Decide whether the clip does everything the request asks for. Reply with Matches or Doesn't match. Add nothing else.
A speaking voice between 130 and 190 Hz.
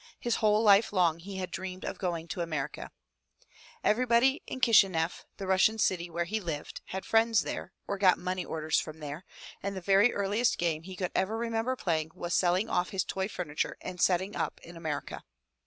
Matches